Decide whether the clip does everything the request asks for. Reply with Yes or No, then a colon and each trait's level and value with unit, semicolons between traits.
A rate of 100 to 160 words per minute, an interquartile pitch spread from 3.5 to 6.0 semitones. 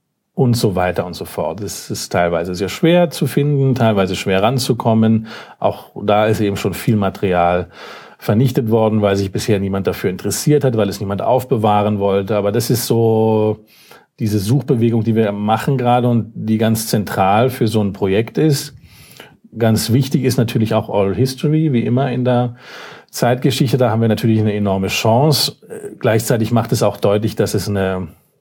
No: average, 175 wpm; average, 3.9 semitones